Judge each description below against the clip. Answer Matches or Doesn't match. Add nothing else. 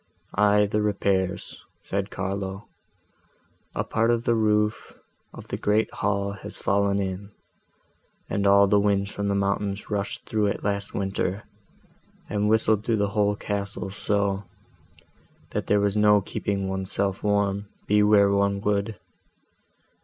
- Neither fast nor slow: Matches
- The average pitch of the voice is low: Matches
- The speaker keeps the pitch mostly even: Matches